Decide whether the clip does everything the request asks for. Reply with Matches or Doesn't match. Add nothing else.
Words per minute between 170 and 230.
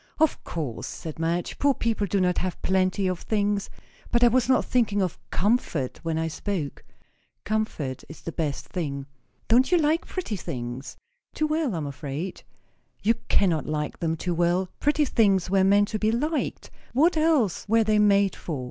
Matches